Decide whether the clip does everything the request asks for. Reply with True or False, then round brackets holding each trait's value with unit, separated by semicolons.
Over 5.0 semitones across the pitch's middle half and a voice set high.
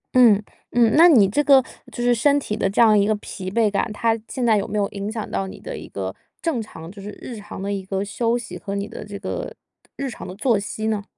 False (3.1 semitones; 210 Hz)